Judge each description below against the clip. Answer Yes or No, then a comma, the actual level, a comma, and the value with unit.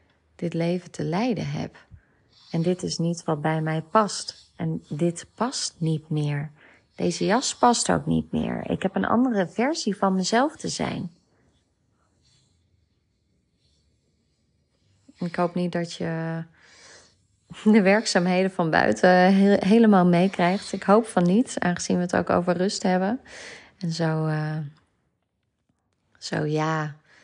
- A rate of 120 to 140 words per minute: Yes, slow, 135 wpm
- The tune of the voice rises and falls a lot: No, average, 4.0 semitones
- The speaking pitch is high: No, medium, 175 Hz